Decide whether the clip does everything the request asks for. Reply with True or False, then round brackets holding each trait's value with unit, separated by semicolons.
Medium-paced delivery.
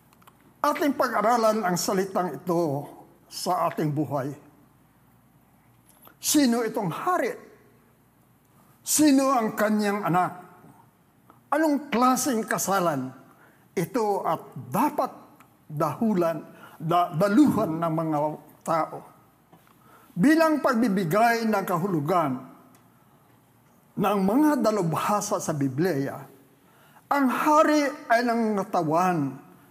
False (80 wpm)